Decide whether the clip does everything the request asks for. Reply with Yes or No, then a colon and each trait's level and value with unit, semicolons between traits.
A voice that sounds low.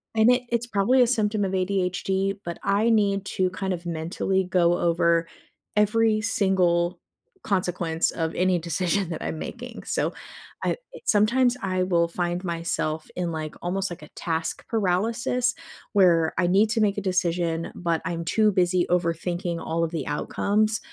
No: medium, 185 Hz